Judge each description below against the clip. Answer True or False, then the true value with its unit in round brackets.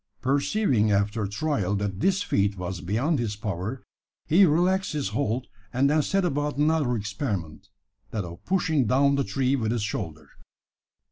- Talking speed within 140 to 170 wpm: True (155 wpm)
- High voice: False (125 Hz)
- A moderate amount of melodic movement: False (6.5 semitones)